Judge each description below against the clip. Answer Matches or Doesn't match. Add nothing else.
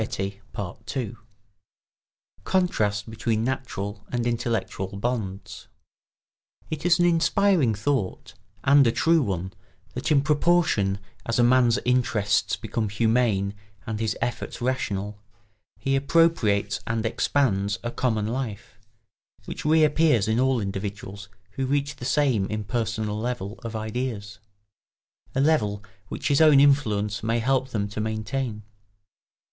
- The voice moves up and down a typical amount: Matches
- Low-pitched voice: Matches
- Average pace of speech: Doesn't match